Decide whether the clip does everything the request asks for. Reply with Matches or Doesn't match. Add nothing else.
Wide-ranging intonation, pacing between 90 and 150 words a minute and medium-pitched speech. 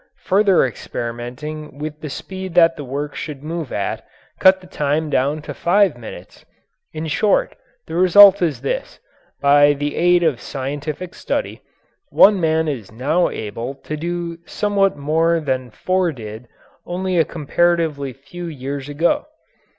Doesn't match